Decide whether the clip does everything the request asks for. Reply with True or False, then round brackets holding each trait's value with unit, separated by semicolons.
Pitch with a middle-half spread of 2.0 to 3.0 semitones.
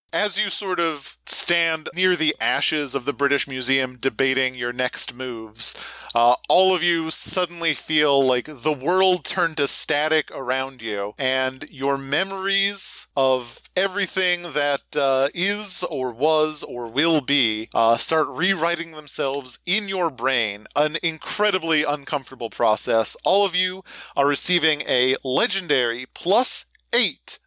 False (5.1 semitones)